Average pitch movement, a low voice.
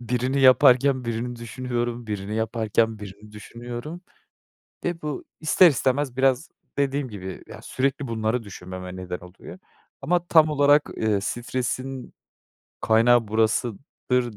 Yes: average, 3.6 semitones; low, 120 Hz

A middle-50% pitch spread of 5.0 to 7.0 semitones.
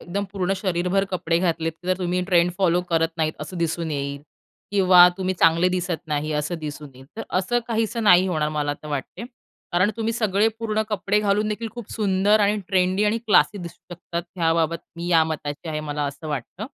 No: average, 3.8 semitones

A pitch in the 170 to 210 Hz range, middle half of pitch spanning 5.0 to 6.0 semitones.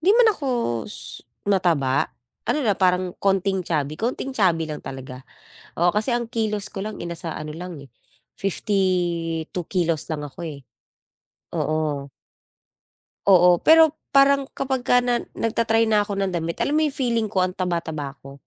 Yes: medium, 185 Hz; wide, 5.6 semitones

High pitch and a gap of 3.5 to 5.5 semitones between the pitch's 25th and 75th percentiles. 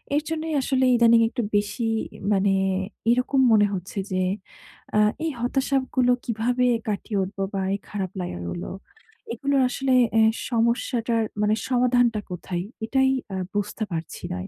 Yes: high, 230 Hz; average, 4.1 semitones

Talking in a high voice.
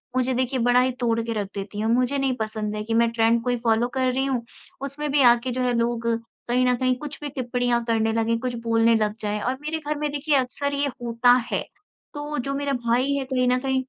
Yes: very high, 250 Hz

